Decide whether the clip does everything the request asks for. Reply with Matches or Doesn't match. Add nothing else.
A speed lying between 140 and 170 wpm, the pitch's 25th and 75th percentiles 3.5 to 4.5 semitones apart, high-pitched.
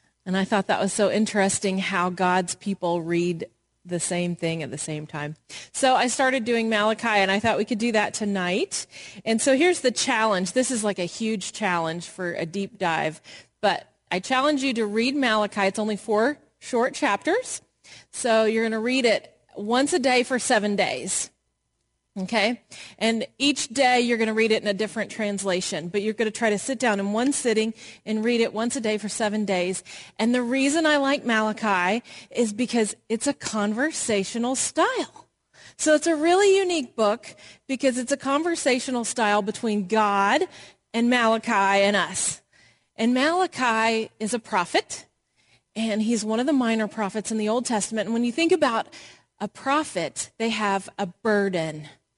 Doesn't match